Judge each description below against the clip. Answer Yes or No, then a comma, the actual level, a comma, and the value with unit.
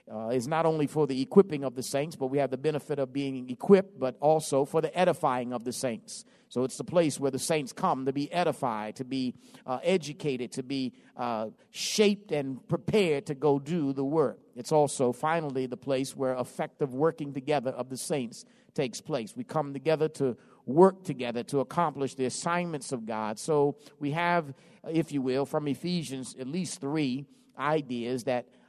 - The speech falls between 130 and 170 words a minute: No, average, 190 wpm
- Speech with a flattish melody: No, average, 3.4 semitones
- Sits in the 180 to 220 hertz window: No, medium, 140 Hz